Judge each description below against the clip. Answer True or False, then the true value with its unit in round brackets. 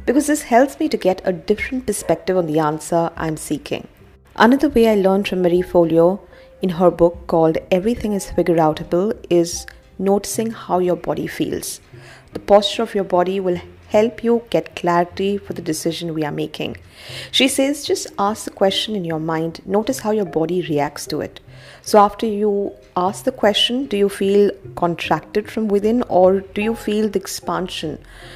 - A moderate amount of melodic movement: True (3.9 semitones)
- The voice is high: True (195 Hz)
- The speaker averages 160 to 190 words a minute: True (180 wpm)